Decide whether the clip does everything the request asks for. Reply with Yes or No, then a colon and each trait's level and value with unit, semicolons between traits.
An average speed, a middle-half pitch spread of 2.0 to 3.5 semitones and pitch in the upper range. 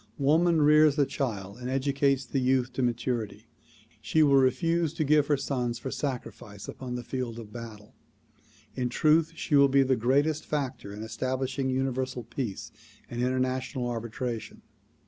No: average, 155 wpm; average, 2.7 semitones; low, 130 Hz